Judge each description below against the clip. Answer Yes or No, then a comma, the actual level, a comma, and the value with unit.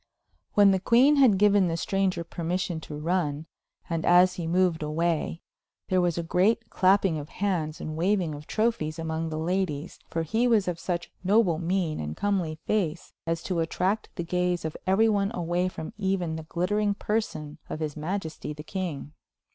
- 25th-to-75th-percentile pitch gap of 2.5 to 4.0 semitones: Yes, average, 3.4 semitones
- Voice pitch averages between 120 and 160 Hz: No, medium, 175 Hz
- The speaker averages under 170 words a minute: No, average, 180 wpm